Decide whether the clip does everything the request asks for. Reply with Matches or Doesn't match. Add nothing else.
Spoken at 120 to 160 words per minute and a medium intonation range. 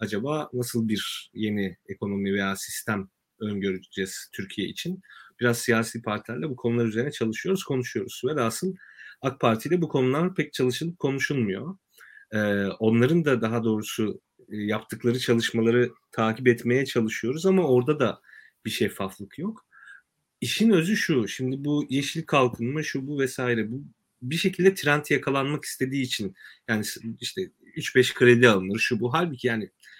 Matches